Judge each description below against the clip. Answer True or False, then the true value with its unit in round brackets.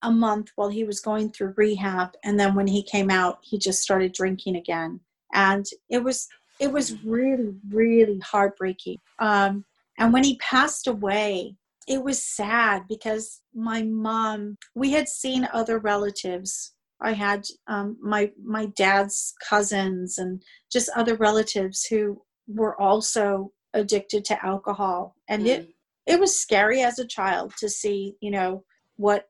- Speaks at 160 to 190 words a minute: False (150 wpm)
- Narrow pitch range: True (2.3 semitones)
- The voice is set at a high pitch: True (210 Hz)